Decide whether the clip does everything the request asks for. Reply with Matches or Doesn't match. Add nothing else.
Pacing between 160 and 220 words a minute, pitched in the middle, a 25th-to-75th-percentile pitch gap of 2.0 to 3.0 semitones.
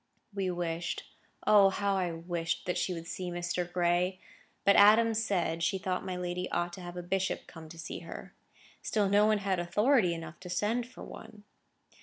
Matches